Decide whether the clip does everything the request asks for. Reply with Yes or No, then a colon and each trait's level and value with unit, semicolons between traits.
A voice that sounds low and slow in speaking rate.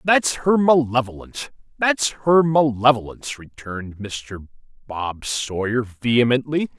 Yes: low, 125 Hz; slow, 90 wpm